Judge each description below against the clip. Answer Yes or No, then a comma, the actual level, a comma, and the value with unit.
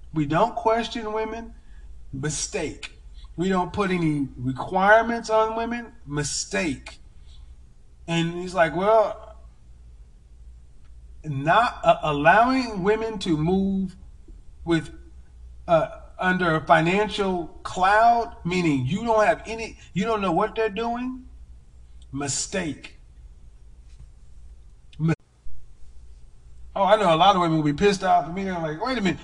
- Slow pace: Yes, slow, 125 wpm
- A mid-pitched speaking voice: Yes, medium, 160 Hz